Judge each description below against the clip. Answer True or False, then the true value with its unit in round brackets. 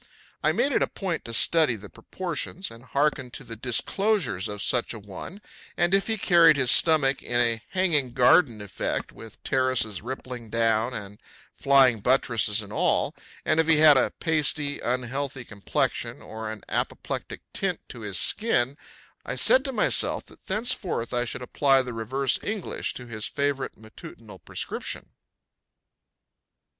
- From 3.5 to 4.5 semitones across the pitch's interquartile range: False (5.5 semitones)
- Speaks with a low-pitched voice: True (130 Hz)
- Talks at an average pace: True (155 wpm)